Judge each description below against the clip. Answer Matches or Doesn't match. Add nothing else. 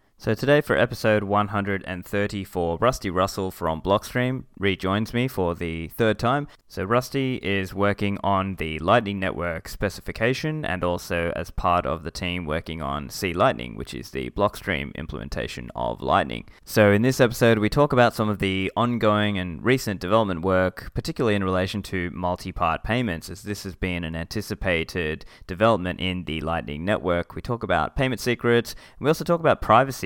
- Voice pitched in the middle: Doesn't match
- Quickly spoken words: Doesn't match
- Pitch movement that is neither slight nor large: Matches